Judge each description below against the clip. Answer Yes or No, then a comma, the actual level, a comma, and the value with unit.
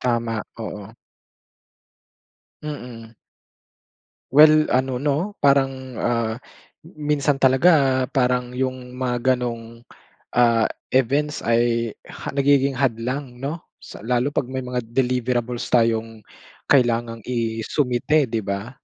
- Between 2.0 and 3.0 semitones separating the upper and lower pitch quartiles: Yes, average, 2.7 semitones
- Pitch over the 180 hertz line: No, low, 125 Hz